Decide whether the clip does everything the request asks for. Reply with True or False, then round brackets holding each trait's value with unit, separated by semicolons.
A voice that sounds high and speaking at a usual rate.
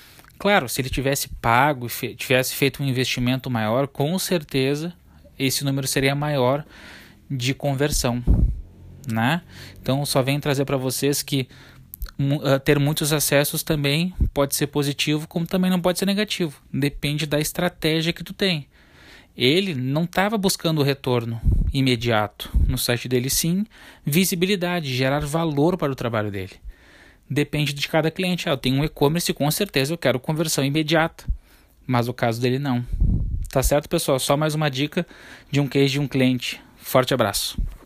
False (140 Hz; 155 wpm)